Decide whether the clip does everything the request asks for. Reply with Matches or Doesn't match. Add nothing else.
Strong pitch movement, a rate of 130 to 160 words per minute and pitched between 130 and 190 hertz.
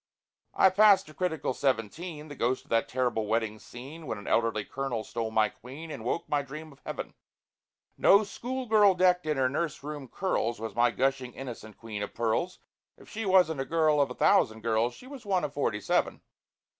Doesn't match